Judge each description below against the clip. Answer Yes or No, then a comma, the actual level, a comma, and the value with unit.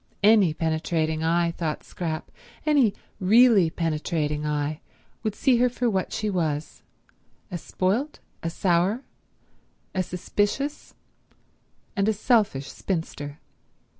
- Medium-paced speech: No, slow, 105 wpm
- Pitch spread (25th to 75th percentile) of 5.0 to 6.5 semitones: Yes, average, 5.3 semitones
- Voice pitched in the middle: Yes, medium, 180 Hz